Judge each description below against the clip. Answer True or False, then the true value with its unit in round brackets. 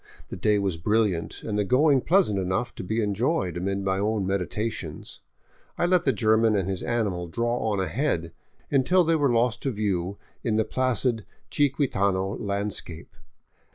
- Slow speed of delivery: False (160 wpm)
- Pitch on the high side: False (105 Hz)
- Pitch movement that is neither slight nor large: True (4.5 semitones)